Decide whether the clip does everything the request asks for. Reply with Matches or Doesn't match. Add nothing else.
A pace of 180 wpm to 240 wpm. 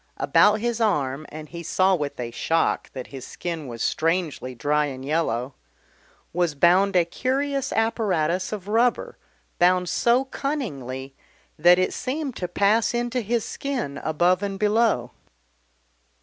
Doesn't match